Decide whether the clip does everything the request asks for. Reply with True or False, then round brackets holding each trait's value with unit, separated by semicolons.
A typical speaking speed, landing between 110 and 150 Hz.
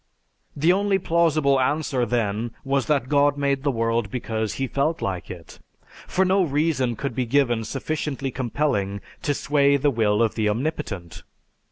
True (160 wpm; 135 Hz)